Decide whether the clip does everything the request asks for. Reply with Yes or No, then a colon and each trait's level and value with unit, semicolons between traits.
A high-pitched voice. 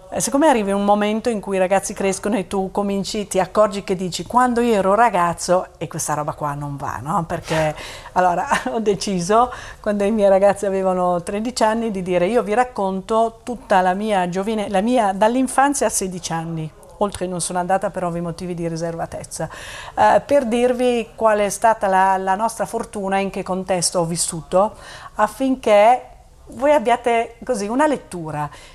Yes: high, 200 Hz